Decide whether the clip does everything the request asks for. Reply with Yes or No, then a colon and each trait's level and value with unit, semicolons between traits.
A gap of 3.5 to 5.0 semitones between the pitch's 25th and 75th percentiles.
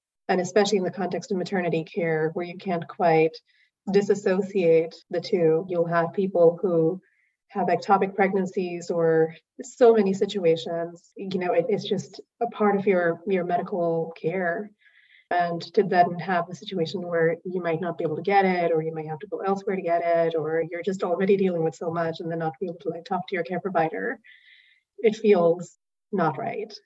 No: average, 2.9 semitones